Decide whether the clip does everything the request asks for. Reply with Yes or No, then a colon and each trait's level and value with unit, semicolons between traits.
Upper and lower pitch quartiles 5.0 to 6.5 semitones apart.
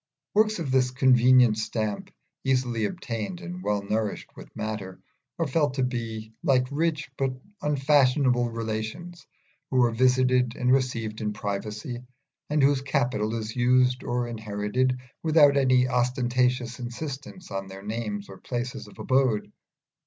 No: average, 3.3 semitones